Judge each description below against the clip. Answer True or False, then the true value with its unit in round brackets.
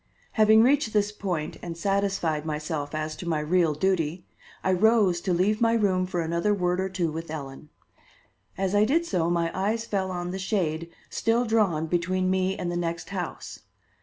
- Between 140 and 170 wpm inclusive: False (185 wpm)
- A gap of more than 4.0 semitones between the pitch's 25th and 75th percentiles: False (3.5 semitones)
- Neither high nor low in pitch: True (180 Hz)